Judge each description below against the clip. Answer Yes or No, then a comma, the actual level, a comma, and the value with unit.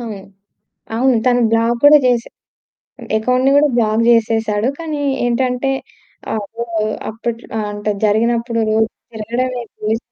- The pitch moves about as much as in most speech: No, narrow, 2.2 semitones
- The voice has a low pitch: No, high, 230 Hz